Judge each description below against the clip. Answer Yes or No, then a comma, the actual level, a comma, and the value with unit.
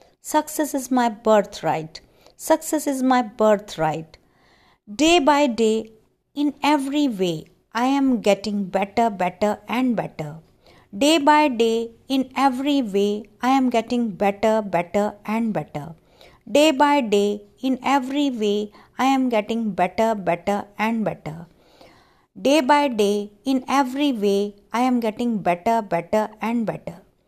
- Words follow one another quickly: No, average, 130 wpm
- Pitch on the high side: Yes, high, 225 Hz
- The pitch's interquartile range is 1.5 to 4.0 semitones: No, average, 4.8 semitones